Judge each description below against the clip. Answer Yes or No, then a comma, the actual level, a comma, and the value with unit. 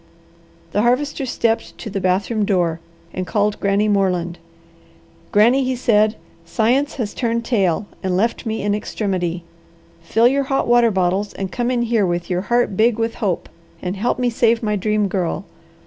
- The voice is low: No, high, 210 Hz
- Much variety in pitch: No, average, 3.8 semitones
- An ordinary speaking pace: Yes, average, 170 wpm